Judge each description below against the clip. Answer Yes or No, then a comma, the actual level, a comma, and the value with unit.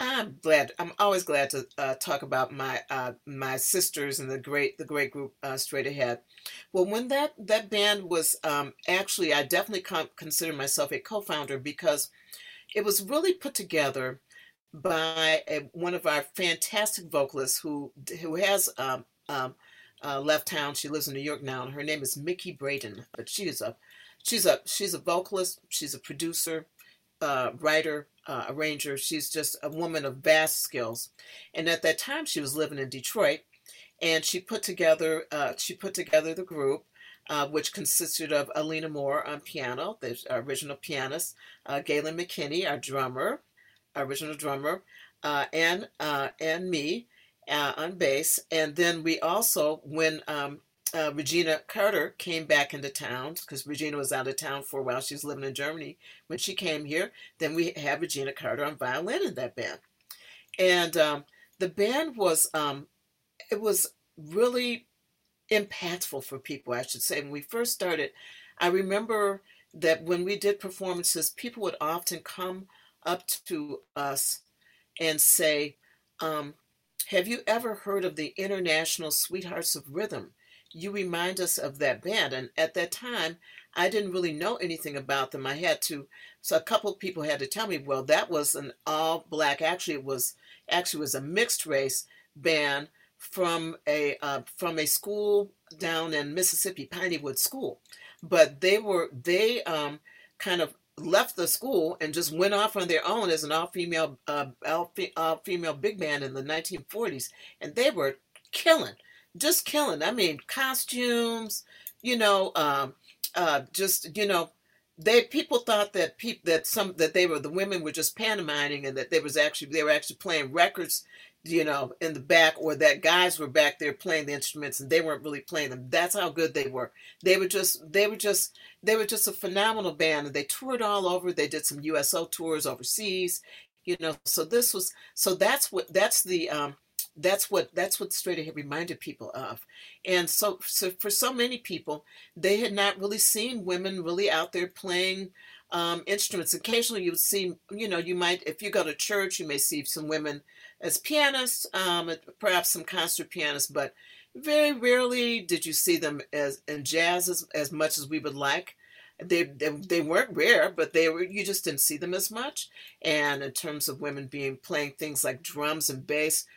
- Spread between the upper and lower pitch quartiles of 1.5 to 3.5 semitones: No, average, 4.7 semitones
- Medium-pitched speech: Yes, medium, 165 Hz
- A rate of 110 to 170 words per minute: No, average, 185 wpm